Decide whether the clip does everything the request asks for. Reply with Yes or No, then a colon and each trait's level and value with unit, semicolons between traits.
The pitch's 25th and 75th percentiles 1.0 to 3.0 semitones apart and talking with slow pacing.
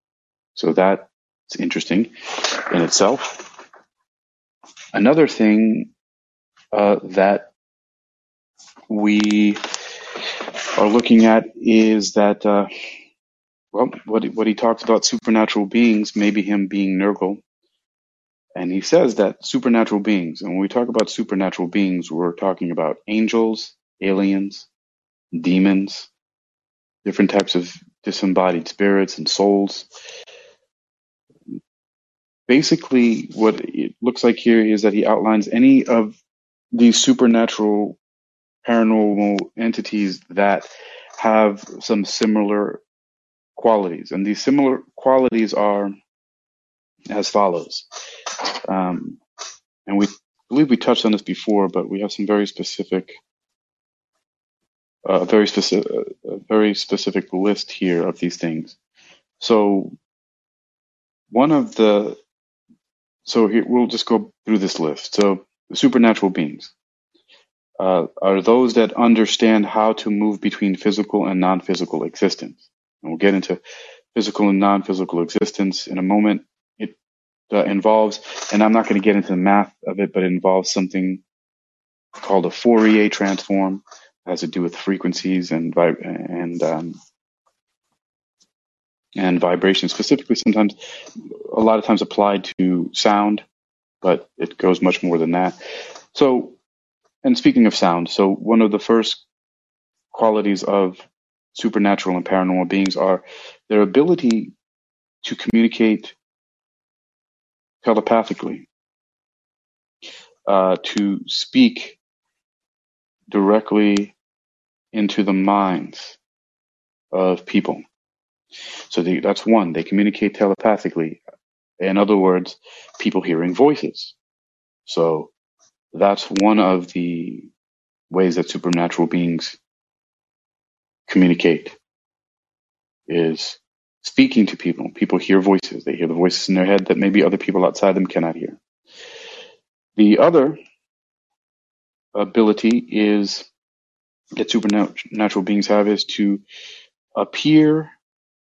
Yes: average, 2.7 semitones; slow, 115 wpm